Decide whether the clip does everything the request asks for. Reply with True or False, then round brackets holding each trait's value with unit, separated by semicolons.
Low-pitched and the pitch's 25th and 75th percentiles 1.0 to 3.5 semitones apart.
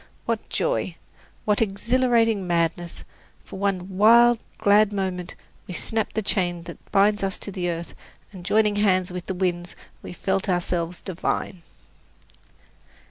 False (190 Hz; 2.9 semitones)